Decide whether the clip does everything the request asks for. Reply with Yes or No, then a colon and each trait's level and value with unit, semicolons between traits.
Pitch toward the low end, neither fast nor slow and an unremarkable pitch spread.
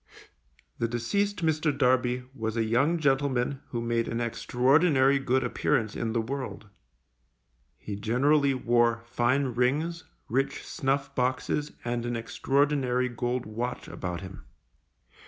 No: low, 125 Hz; slow, 125 wpm; average, 3.0 semitones